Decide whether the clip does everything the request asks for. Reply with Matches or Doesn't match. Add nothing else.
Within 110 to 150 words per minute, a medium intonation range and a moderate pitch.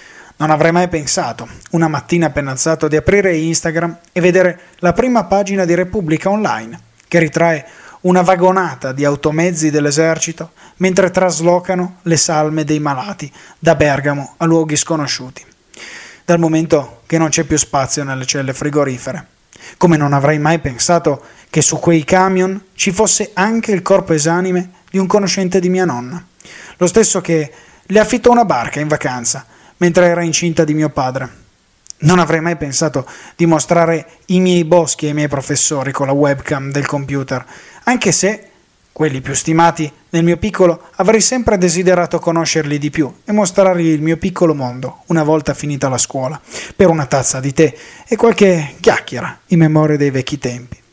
Doesn't match